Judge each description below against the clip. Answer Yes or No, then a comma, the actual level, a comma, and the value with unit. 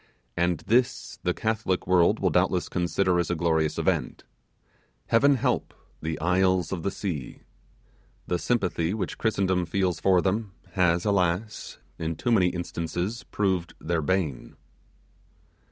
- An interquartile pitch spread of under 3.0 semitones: Yes, narrow, 2.6 semitones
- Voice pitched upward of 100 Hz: No, very low, 90 Hz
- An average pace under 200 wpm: Yes, slow, 135 wpm